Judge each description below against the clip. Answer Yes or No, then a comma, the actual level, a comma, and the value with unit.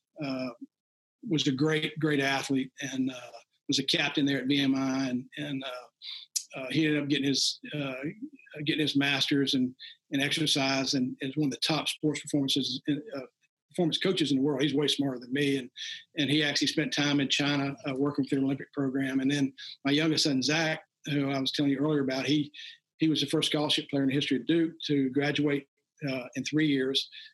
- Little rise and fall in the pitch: Yes, narrow, 2.0 semitones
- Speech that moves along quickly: Yes, fast, 210 wpm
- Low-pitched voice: No, medium, 145 Hz